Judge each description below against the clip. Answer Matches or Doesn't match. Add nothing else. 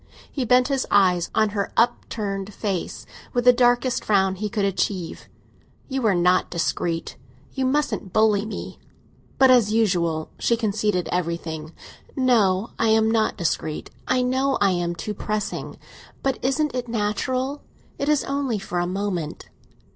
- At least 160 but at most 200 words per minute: Doesn't match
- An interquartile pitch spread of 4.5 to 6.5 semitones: Matches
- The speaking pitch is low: Doesn't match